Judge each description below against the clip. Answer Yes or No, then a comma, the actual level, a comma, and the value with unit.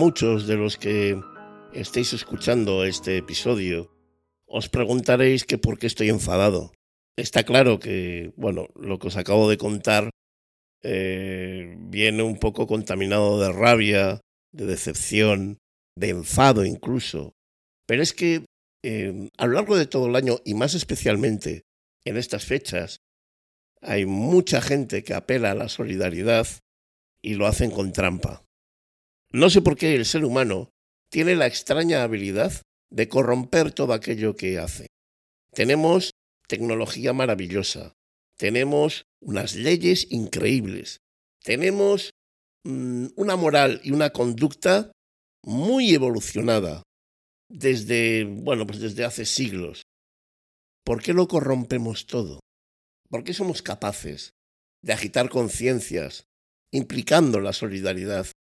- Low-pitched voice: Yes, low, 110 Hz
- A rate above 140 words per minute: No, slow, 125 wpm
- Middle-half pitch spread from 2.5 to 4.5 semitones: No, wide, 5.4 semitones